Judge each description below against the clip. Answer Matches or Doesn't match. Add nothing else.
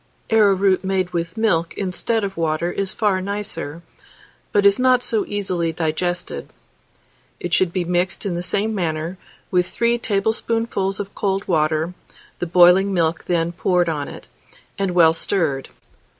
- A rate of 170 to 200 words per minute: Doesn't match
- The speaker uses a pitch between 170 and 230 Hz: Matches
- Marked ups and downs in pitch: Doesn't match